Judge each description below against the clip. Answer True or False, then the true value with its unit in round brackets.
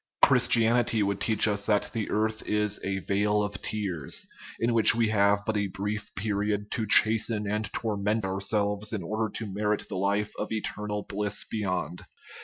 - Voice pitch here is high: False (105 Hz)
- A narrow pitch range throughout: True (1.3 semitones)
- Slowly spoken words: False (170 wpm)